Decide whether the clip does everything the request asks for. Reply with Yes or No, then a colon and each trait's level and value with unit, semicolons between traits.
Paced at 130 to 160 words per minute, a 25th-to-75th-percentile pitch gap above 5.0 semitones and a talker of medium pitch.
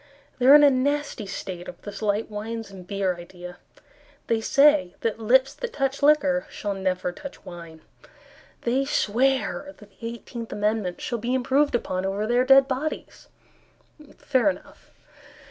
No: average, 155 wpm; wide, 5.5 semitones; high, 230 Hz